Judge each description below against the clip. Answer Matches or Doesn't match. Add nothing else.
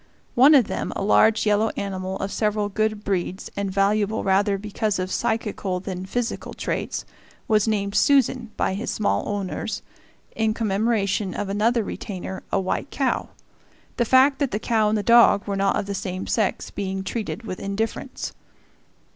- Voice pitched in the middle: Doesn't match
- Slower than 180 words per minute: Matches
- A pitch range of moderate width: Doesn't match